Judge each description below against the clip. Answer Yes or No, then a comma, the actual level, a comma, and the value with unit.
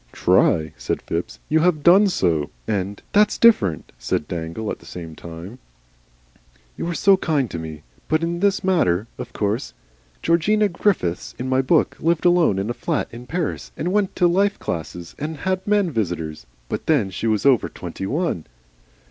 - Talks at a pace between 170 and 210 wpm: Yes, average, 175 wpm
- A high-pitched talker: No, low, 130 Hz